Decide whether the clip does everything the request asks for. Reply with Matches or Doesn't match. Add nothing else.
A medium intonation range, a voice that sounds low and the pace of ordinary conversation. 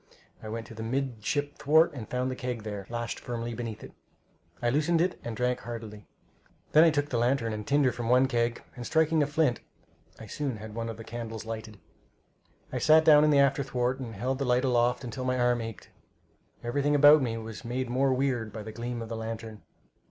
Doesn't match